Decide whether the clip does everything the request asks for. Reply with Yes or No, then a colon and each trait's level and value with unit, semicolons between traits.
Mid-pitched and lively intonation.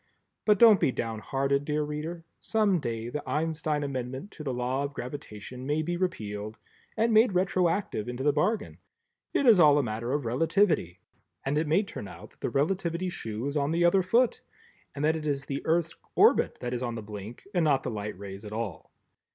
Yes: medium, 145 Hz; wide, 6.0 semitones